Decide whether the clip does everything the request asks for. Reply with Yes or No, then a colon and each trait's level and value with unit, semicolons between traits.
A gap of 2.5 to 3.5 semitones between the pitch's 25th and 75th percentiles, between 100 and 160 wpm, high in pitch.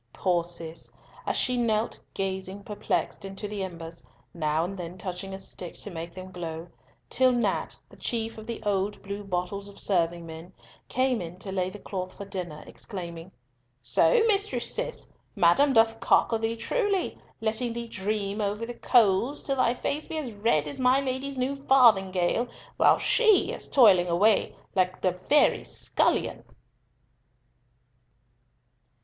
No: average, 4.9 semitones; average, 155 wpm; high, 200 Hz